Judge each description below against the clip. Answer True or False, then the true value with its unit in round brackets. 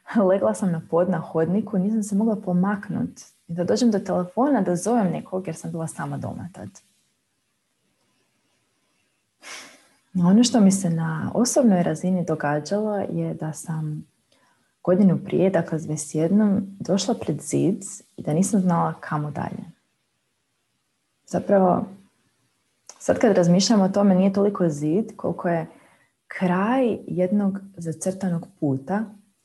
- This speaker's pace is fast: False (130 wpm)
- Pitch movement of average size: True (3.4 semitones)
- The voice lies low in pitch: False (185 Hz)